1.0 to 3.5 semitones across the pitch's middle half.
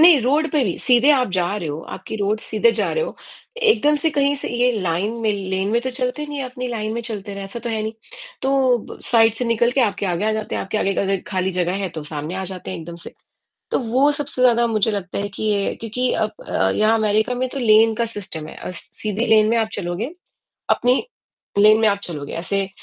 No: average, 4.3 semitones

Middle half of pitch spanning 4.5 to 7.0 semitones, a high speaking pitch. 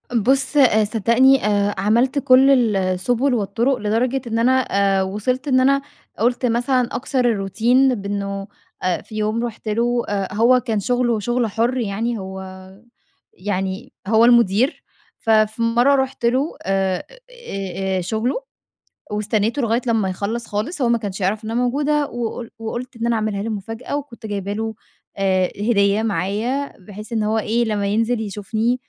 No: average, 3.4 semitones; high, 225 Hz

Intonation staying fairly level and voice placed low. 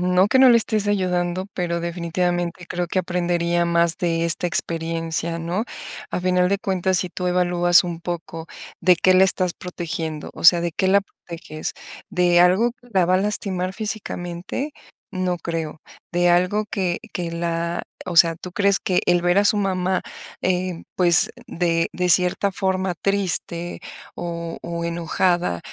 No: narrow, 1.6 semitones; medium, 175 Hz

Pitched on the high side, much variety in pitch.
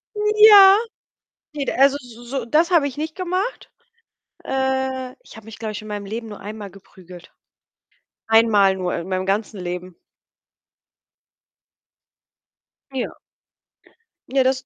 Yes: high, 235 Hz; wide, 5.8 semitones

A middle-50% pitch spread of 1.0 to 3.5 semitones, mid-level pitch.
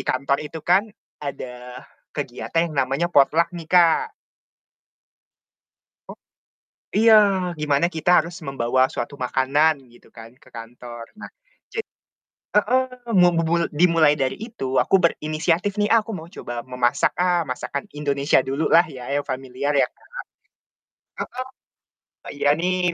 No: average, 5.1 semitones; medium, 155 Hz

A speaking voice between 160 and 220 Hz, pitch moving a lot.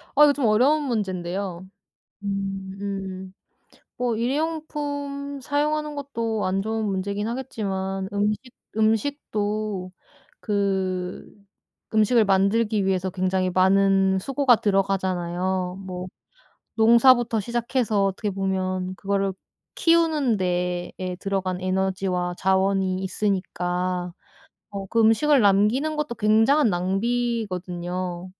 No: high, 200 Hz; average, 3.9 semitones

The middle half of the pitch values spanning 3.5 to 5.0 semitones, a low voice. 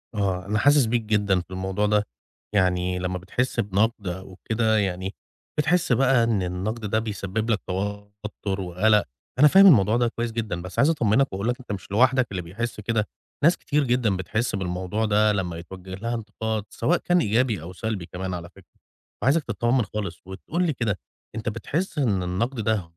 Yes: average, 3.9 semitones; low, 105 Hz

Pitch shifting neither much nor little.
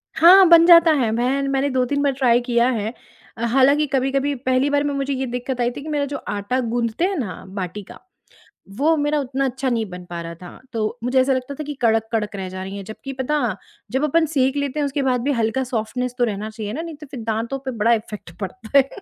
Yes: average, 4.0 semitones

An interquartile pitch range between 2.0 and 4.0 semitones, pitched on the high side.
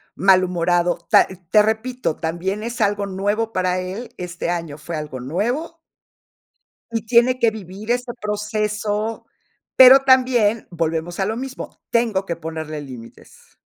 No: average, 4.9 semitones; high, 205 Hz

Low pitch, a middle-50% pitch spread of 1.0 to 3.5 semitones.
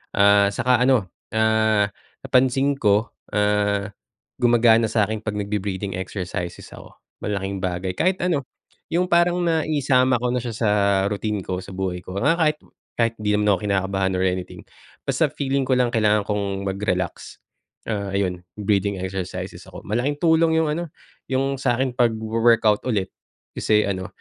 No: low, 105 Hz; average, 4.4 semitones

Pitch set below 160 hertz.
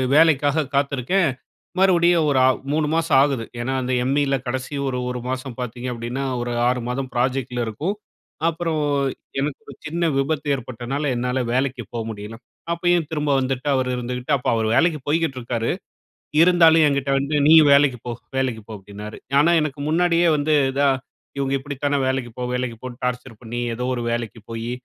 Yes: low, 135 Hz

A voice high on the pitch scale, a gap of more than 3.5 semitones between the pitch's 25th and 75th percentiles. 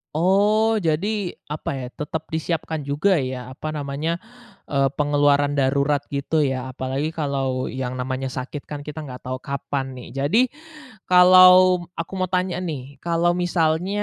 No: medium, 150 Hz; average, 4.0 semitones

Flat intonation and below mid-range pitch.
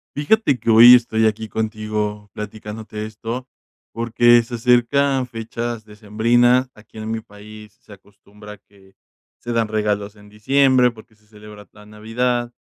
Yes: narrow, 2.2 semitones; low, 110 Hz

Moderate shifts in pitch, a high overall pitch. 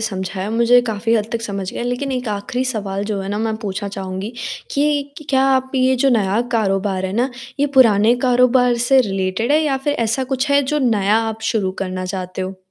Yes: average, 4.5 semitones; high, 220 Hz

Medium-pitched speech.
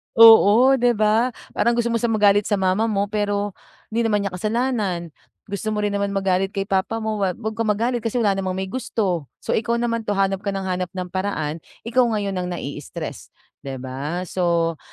No: high, 200 Hz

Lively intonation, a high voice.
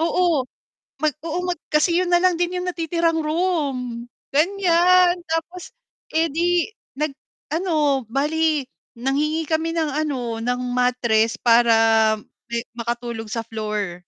Yes: wide, 5.8 semitones; very high, 305 Hz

